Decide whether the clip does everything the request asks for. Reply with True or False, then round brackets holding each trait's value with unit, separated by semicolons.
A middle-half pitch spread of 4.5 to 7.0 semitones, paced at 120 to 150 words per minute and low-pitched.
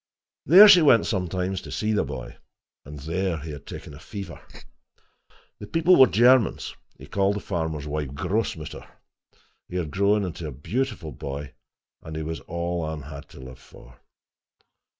False (5.6 semitones; 165 wpm; 85 Hz)